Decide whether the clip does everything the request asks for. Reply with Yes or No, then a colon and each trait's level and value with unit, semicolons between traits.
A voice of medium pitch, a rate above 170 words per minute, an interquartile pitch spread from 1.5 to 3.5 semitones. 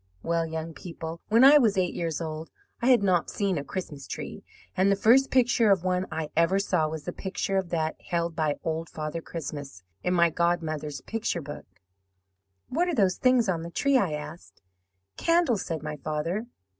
No: medium, 170 Hz; average, 190 wpm; average, 4.1 semitones